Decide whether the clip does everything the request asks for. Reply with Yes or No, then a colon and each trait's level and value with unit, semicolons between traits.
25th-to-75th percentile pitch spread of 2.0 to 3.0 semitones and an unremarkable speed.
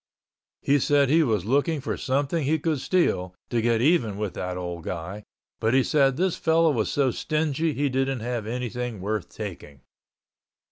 No: average, 5.3 semitones; average, 175 wpm